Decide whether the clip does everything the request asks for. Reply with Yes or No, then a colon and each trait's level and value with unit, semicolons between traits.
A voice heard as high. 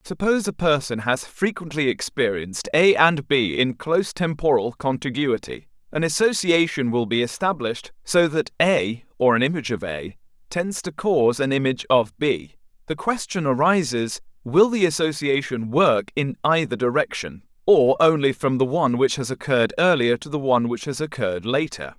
No: medium, 140 Hz